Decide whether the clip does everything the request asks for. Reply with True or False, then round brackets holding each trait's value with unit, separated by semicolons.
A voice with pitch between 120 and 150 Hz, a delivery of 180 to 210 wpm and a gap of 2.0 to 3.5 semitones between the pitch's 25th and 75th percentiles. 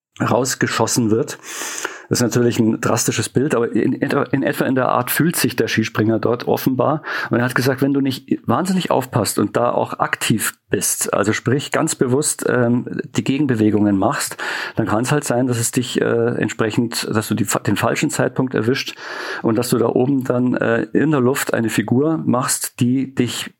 True (125 Hz; 190 wpm; 2.6 semitones)